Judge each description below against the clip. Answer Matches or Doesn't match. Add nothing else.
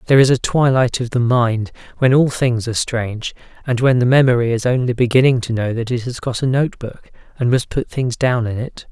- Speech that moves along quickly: Matches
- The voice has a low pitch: Matches